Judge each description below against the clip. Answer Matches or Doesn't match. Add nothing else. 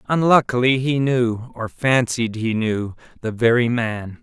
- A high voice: Doesn't match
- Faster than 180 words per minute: Doesn't match